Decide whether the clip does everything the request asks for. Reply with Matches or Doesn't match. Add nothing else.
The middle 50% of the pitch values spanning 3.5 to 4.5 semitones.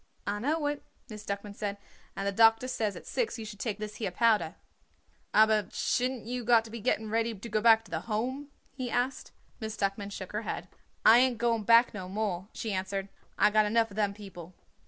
Doesn't match